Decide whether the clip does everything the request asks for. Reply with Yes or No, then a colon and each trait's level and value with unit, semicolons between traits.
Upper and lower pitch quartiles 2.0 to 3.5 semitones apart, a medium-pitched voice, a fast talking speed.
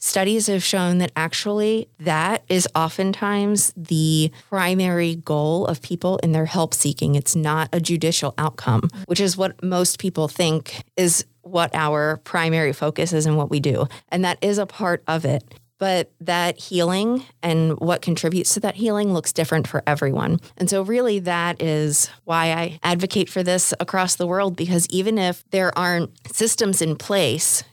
No: average, 3.0 semitones; medium, 170 Hz; average, 170 wpm